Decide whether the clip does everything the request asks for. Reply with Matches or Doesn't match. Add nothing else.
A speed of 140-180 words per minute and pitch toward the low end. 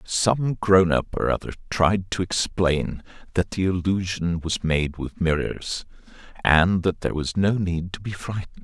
Matches